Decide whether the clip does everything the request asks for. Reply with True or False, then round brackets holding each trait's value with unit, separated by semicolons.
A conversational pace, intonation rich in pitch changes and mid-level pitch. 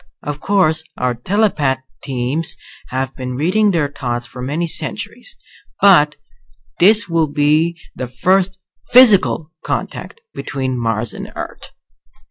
False (120 wpm; 6.0 semitones; 150 Hz)